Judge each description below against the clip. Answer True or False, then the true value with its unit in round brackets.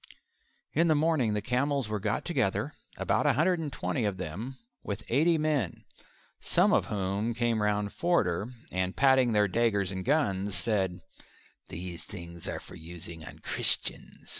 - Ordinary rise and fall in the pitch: False (6.3 semitones)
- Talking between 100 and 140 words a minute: False (160 wpm)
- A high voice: False (105 Hz)